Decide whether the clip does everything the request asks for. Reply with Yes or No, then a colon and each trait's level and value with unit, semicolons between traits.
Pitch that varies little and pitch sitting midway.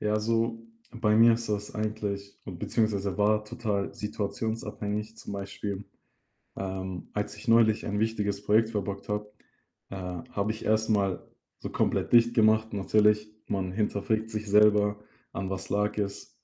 No: narrow, 1.5 semitones; low, 105 Hz